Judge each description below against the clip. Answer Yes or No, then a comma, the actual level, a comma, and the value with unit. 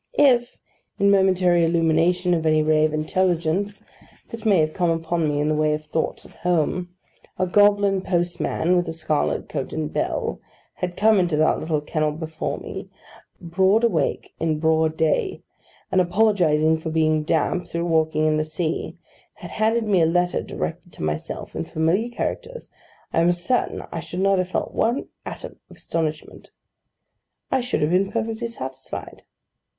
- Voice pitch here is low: No, medium, 170 Hz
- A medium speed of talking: Yes, average, 170 wpm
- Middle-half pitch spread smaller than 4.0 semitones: Yes, average, 3.5 semitones